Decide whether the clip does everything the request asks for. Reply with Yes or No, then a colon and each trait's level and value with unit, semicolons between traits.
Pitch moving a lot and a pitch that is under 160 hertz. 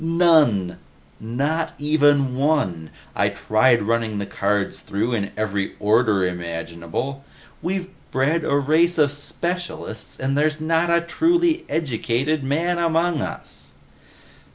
Yes: wide, 7.1 semitones; medium, 140 Hz